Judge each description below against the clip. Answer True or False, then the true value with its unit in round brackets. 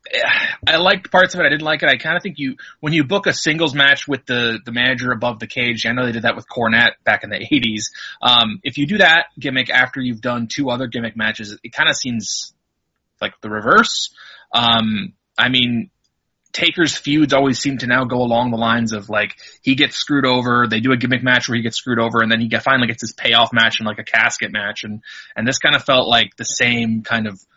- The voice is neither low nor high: False (120 Hz)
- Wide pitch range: False (2.7 semitones)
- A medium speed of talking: False (240 wpm)